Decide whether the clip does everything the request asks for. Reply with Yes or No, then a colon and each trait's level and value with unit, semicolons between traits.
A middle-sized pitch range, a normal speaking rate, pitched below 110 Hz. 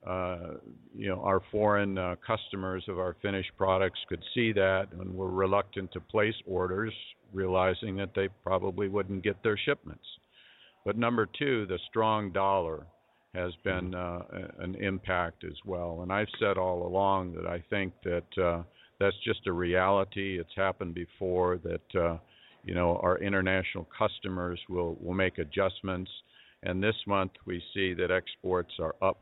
No: narrow, 1.6 semitones; average, 160 wpm; very low, 95 Hz